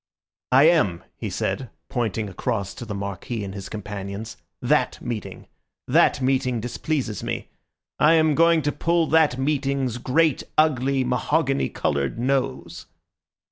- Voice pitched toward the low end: Yes, low, 130 Hz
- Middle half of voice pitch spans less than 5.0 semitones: No, wide, 5.6 semitones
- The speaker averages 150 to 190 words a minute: No, slow, 135 wpm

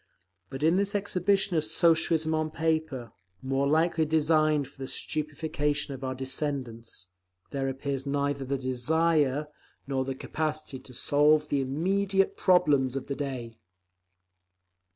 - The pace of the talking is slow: Yes, slow, 125 wpm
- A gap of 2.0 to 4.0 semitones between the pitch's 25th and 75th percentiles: Yes, average, 3.1 semitones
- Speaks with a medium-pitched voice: Yes, medium, 145 Hz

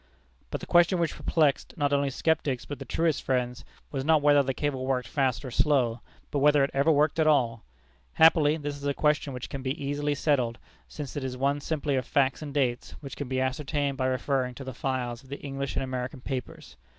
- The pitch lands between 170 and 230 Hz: No, medium, 140 Hz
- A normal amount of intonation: No, narrow, 2.1 semitones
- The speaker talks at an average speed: No, fast, 220 wpm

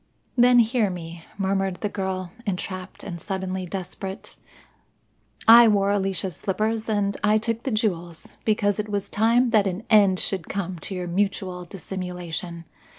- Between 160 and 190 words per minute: No, average, 150 wpm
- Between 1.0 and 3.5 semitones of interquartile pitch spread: Yes, average, 2.7 semitones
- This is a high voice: Yes, high, 195 Hz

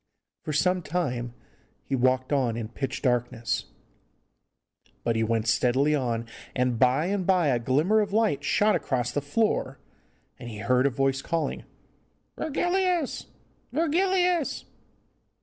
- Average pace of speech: No, slow, 130 wpm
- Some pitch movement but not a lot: No, wide, 8.5 semitones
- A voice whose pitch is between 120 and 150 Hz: Yes, medium, 140 Hz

